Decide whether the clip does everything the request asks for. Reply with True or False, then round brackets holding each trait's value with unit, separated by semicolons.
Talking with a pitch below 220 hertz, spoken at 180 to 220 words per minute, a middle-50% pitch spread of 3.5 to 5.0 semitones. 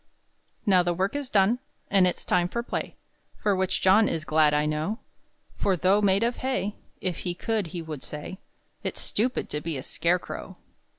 True (185 Hz; 185 wpm; 4.1 semitones)